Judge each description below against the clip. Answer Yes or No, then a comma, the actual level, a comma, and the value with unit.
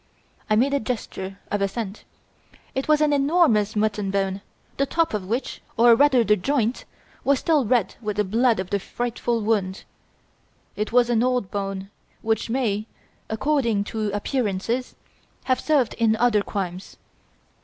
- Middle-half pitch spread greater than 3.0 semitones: Yes, average, 3.9 semitones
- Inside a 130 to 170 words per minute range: Yes, average, 155 wpm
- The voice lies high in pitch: Yes, high, 225 Hz